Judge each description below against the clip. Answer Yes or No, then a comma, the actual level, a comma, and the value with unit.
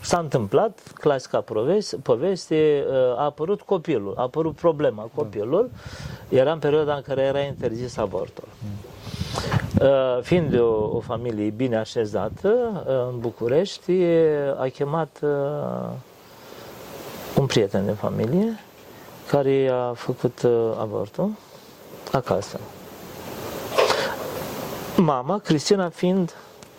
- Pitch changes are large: Yes, wide, 6.0 semitones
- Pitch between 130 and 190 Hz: Yes, medium, 140 Hz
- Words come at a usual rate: No, slow, 90 wpm